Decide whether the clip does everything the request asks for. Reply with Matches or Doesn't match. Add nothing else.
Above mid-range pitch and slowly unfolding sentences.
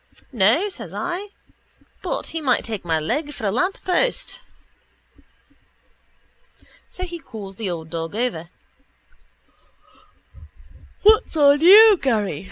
Matches